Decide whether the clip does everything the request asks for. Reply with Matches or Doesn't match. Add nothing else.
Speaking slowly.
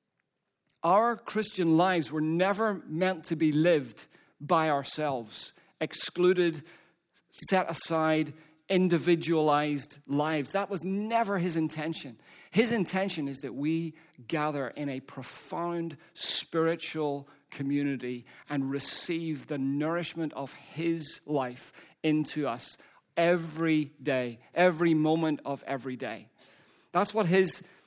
Matches